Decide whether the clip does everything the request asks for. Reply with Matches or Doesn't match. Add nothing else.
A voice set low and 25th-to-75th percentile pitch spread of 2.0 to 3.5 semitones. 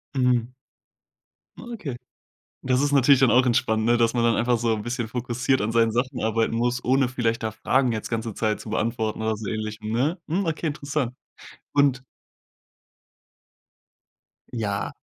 Matches